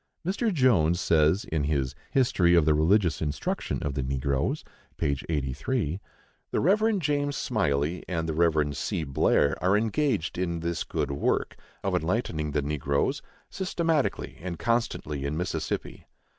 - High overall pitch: No, very low, 80 Hz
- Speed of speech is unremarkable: Yes, average, 145 wpm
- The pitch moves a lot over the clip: Yes, wide, 7.6 semitones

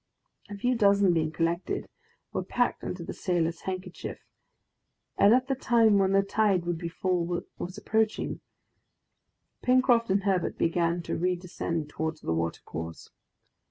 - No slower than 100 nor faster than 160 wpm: Yes, average, 140 wpm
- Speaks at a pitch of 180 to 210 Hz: Yes, medium, 185 Hz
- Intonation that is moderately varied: Yes, average, 3.7 semitones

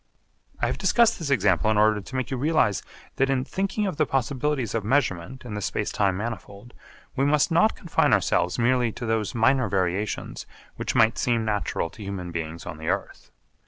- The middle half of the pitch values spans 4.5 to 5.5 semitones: Yes, average, 5.1 semitones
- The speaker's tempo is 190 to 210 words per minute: Yes, average, 195 wpm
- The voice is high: No, low, 115 Hz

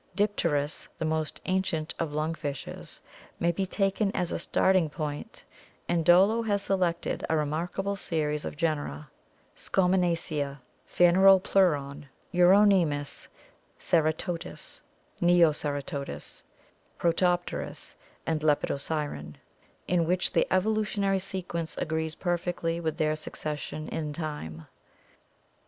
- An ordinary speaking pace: No, slow, 105 wpm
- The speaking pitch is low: No, medium, 165 Hz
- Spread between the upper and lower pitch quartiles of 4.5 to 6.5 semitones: No, average, 3.4 semitones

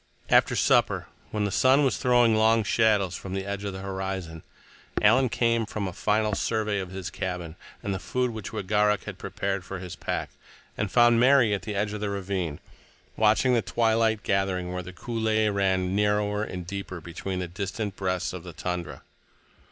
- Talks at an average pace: Yes, average, 185 wpm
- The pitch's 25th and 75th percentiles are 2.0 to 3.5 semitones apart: Yes, average, 2.9 semitones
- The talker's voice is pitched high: No, low, 100 Hz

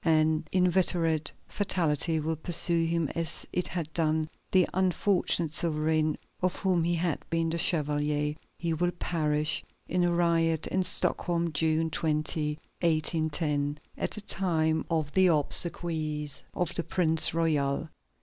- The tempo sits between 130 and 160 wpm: Yes, slow, 135 wpm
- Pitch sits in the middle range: Yes, medium, 165 Hz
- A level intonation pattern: Yes, narrow, 2.0 semitones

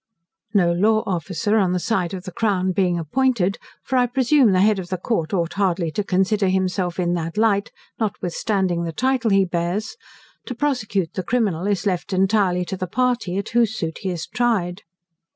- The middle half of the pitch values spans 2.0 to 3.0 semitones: No, average, 3.6 semitones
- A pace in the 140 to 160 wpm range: No, average, 190 wpm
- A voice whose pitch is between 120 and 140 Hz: No, high, 190 Hz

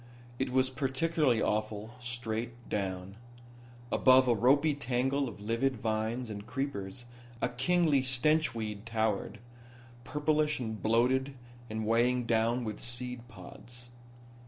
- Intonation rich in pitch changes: No, average, 3.0 semitones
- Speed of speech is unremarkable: No, slow, 120 wpm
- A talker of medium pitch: No, low, 120 Hz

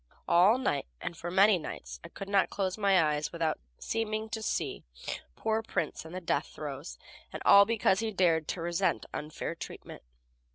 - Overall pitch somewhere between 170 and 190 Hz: Yes, medium, 185 Hz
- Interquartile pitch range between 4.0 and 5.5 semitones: Yes, average, 4.3 semitones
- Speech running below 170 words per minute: No, average, 175 wpm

